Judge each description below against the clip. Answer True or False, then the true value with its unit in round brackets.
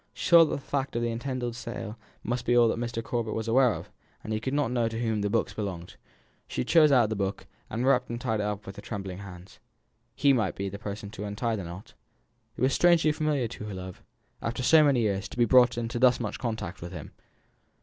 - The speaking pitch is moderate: False (115 Hz)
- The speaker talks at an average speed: False (240 wpm)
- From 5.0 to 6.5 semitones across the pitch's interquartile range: False (3.6 semitones)